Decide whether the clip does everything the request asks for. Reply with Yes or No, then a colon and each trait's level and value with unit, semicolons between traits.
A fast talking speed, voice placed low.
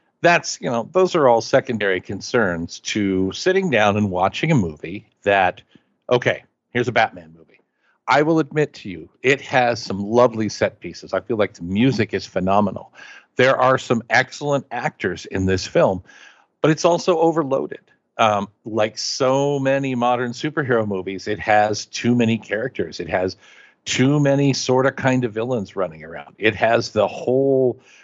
No: average, 165 wpm; low, 125 Hz